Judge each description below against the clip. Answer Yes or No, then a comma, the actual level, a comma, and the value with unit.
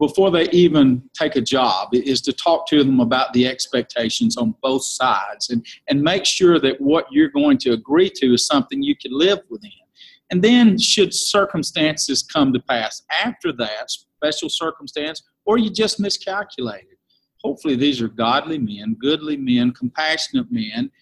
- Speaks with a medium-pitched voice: Yes, medium, 170 Hz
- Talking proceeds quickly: No, average, 165 wpm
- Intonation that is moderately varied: No, wide, 8.2 semitones